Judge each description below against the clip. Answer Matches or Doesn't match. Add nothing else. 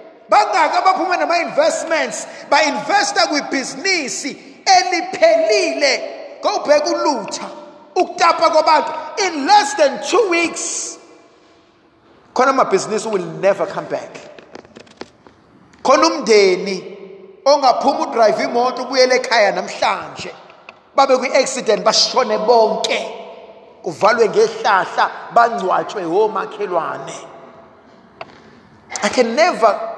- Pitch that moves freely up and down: Matches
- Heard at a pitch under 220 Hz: Doesn't match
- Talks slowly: Matches